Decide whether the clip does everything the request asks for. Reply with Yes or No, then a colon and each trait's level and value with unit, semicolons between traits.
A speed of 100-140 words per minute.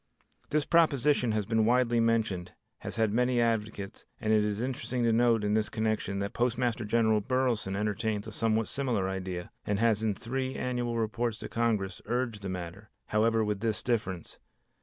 No: average, 175 wpm